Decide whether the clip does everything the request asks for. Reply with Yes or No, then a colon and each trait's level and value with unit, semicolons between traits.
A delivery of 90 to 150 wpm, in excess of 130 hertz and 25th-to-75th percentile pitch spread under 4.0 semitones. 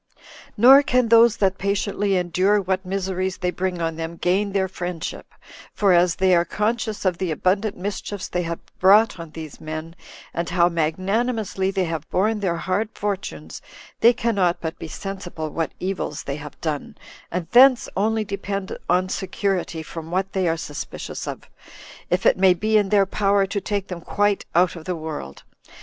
No: average, 175 wpm; medium, 185 Hz; average, 3.1 semitones